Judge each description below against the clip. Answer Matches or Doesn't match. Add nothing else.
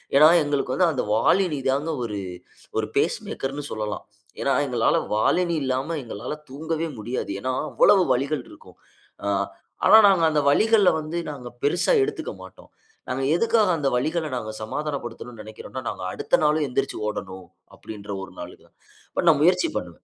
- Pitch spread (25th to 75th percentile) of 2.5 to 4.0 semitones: Doesn't match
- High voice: Doesn't match